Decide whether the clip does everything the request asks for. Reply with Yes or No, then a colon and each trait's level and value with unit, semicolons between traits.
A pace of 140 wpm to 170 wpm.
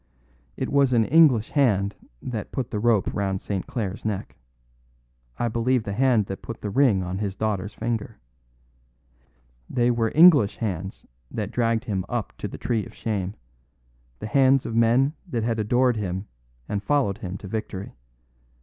Yes: average, 165 wpm